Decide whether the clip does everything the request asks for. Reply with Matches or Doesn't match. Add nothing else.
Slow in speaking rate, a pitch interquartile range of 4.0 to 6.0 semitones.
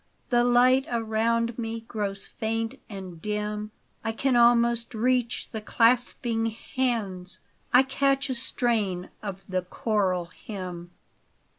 Doesn't match